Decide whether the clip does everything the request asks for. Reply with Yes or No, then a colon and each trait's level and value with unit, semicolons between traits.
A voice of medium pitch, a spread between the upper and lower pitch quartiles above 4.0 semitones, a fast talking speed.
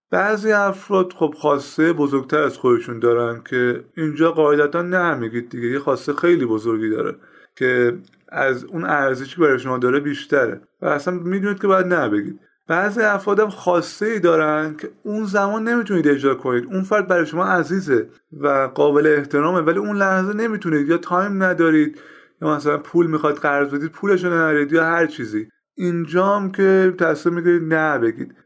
Yes: medium, 165 Hz; average, 4.5 semitones; fast, 160 wpm